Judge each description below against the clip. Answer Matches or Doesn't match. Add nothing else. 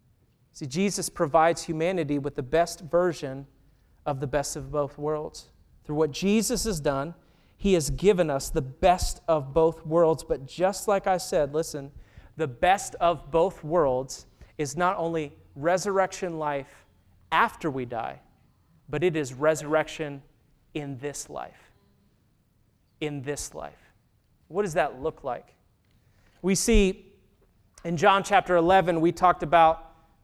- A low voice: Doesn't match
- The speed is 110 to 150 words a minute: Matches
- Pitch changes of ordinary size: Matches